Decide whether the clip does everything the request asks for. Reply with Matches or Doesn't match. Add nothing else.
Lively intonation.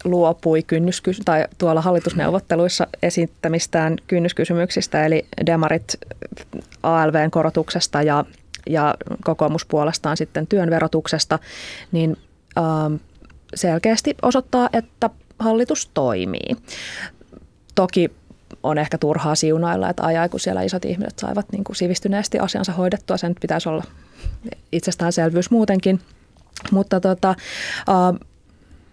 Doesn't match